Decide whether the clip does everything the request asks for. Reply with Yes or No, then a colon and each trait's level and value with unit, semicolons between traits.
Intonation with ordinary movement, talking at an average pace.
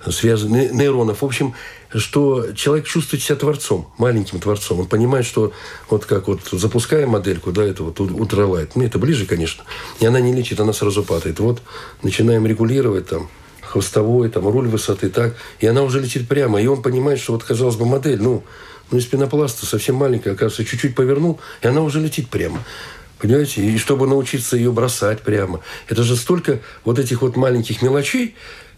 No: average, 4.3 semitones; fast, 180 wpm